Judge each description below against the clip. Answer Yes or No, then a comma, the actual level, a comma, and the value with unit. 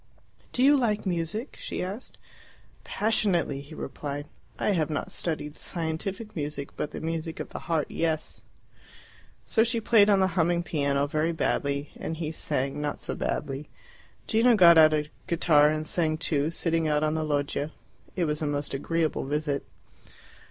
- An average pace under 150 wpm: No, average, 165 wpm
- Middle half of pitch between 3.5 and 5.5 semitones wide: No, average, 3.0 semitones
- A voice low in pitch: No, medium, 160 Hz